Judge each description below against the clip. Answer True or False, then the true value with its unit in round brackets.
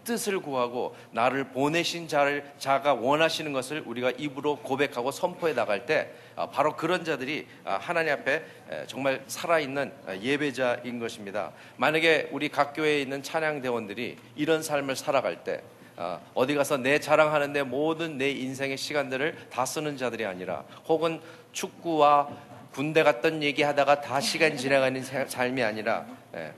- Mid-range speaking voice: True (145 Hz)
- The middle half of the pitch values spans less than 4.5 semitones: True (2.7 semitones)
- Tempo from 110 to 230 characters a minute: False (320 characters per minute)